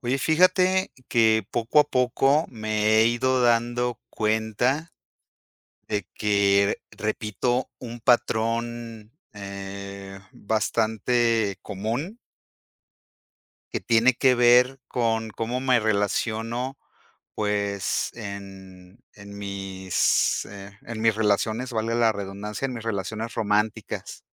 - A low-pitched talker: Yes, low, 110 Hz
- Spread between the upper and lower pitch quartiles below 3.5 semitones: Yes, average, 3.0 semitones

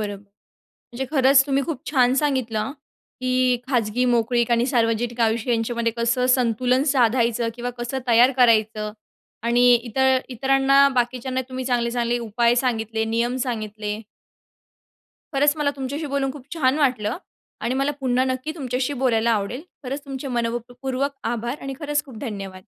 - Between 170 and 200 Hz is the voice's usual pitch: No, high, 245 Hz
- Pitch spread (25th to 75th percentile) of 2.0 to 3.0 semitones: Yes, narrow, 2.4 semitones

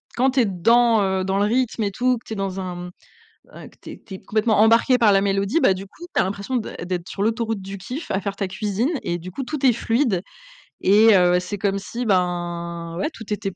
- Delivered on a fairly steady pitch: No, average, 3.5 semitones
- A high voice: Yes, high, 200 Hz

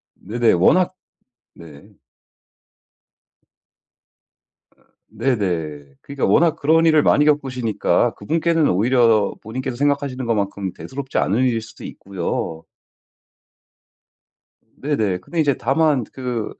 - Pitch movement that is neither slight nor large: No, wide, 6.1 semitones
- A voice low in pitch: Yes, low, 125 Hz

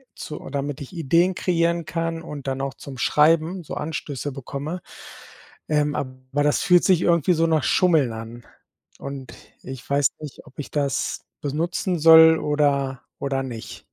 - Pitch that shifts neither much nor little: Yes, average, 3.4 semitones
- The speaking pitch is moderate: Yes, medium, 150 Hz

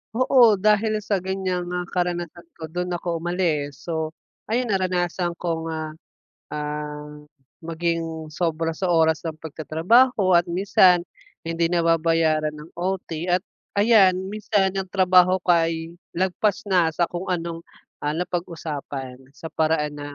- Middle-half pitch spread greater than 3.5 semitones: No, narrow, 2.5 semitones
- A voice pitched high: No, medium, 170 Hz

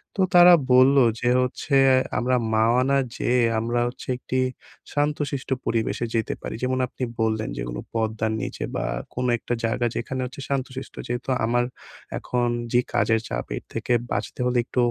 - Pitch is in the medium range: No, low, 125 Hz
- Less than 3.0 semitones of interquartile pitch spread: Yes, narrow, 2.4 semitones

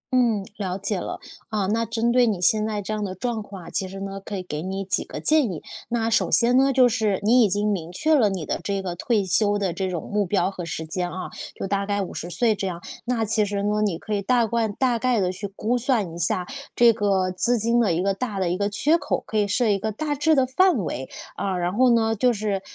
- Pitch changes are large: No, average, 3.5 semitones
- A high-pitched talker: Yes, high, 205 Hz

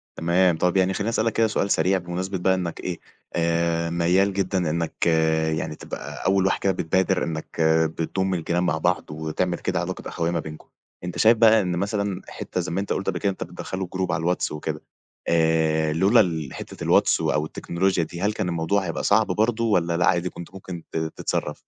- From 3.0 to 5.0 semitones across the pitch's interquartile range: No, narrow, 2.6 semitones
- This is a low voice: Yes, very low, 90 Hz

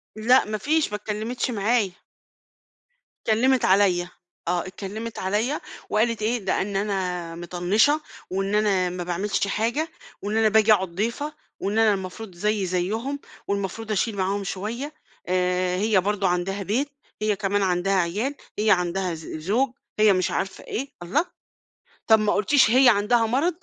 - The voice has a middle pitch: No, high, 205 Hz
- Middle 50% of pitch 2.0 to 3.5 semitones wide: Yes, average, 3.2 semitones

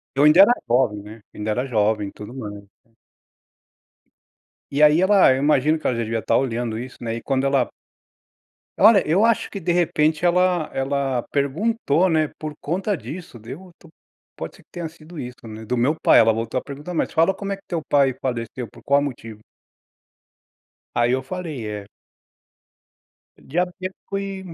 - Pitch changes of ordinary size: No, wide, 6.7 semitones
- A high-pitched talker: No, medium, 140 Hz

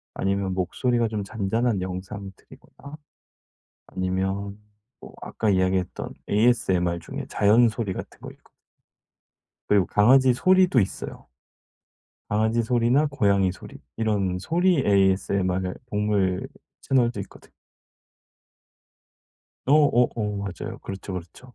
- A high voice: No, low, 100 Hz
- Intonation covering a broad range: No, average, 4.0 semitones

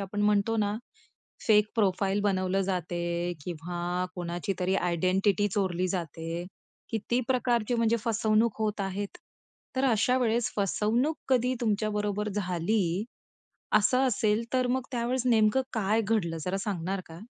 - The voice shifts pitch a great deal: No, average, 3.6 semitones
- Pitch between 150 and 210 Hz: Yes, high, 205 Hz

